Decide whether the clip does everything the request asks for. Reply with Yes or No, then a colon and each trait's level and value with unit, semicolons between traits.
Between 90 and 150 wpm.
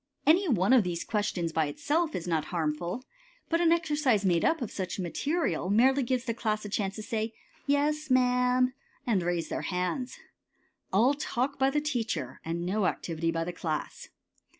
No: average, 175 wpm